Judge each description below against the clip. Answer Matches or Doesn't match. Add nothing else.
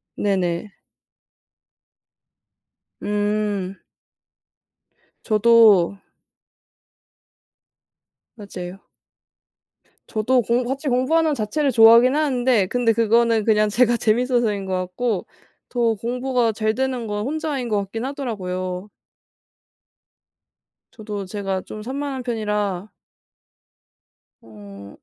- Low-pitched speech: Doesn't match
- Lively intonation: Doesn't match